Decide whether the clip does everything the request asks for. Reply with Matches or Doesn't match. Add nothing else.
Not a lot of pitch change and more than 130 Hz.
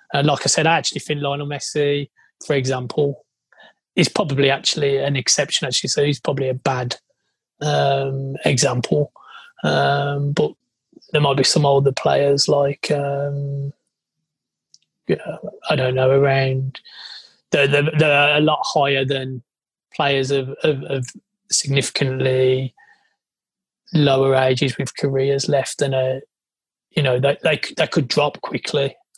Matches